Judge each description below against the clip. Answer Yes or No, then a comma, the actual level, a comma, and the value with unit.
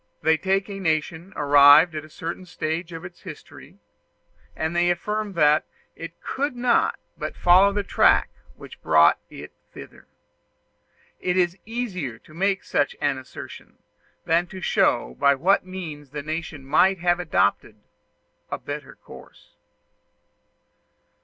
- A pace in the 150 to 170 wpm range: No, average, 140 wpm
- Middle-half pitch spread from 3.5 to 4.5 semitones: Yes, average, 3.8 semitones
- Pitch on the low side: No, medium, 170 Hz